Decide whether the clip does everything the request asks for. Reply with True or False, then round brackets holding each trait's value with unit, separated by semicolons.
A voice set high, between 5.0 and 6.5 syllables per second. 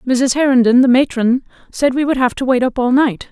True (255 Hz; 5.2 syllables/s)